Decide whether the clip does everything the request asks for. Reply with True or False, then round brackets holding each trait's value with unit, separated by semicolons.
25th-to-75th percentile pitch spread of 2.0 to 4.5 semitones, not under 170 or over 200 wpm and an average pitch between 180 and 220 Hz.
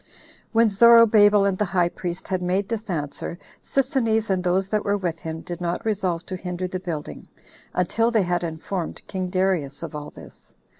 True (3.0 semitones; 190 wpm; 185 Hz)